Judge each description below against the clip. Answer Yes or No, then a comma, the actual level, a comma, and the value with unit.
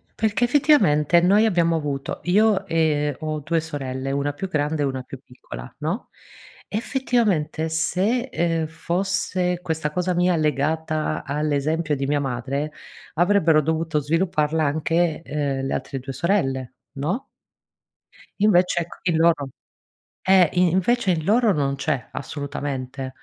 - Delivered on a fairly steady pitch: No, average, 3.9 semitones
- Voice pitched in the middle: Yes, medium, 160 Hz